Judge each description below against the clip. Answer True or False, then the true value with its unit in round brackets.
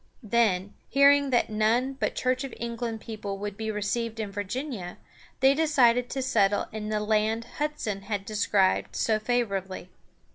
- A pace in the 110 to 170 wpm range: True (150 wpm)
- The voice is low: False (220 Hz)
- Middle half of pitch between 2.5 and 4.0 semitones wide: True (3.3 semitones)